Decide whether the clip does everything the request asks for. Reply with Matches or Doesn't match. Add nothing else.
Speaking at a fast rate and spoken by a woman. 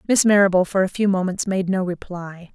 Matches